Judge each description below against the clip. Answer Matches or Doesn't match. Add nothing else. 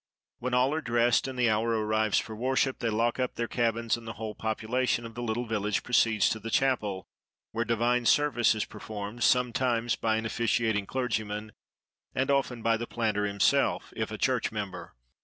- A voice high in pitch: Doesn't match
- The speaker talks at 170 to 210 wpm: Matches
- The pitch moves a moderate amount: Doesn't match